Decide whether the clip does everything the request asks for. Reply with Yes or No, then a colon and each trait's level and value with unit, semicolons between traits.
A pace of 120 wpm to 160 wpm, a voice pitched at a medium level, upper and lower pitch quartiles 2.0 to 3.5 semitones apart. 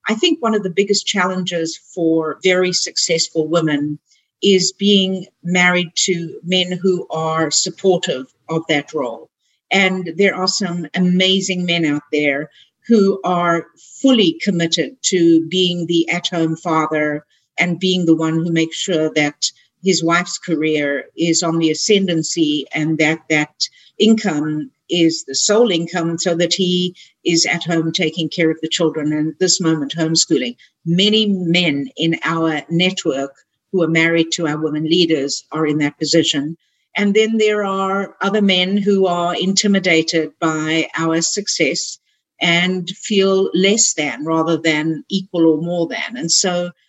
Yes: average, 150 wpm; medium, 170 Hz; average, 2.7 semitones